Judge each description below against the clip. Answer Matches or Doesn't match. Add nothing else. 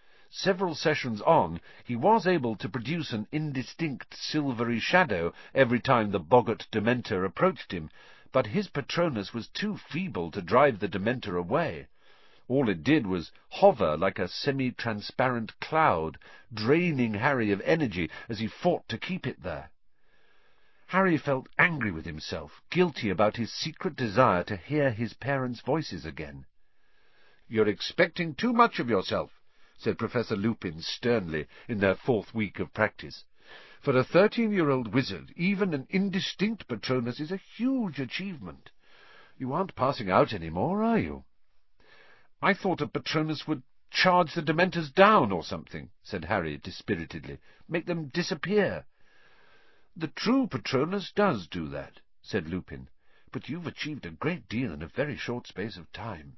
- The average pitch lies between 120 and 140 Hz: Matches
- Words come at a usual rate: Matches